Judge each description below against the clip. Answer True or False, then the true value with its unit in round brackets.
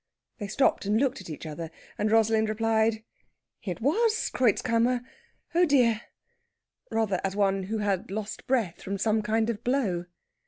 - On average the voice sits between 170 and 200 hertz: False (220 Hz)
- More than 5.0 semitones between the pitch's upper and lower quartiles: False (3.0 semitones)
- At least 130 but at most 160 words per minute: True (155 wpm)